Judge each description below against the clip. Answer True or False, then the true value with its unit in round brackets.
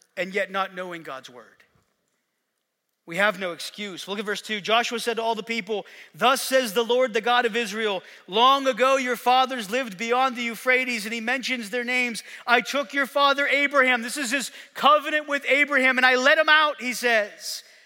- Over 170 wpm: True (200 wpm)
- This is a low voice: False (245 Hz)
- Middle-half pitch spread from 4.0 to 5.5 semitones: False (3.2 semitones)